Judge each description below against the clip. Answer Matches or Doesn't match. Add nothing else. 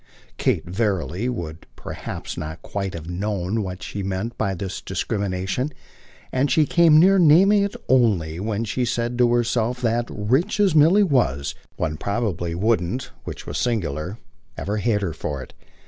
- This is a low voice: Matches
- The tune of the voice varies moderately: Doesn't match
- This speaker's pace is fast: Doesn't match